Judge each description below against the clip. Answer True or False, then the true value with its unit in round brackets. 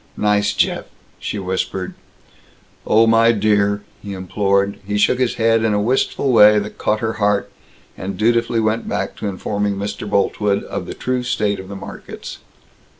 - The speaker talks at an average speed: True (165 wpm)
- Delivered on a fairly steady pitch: True (2.0 semitones)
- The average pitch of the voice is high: False (105 Hz)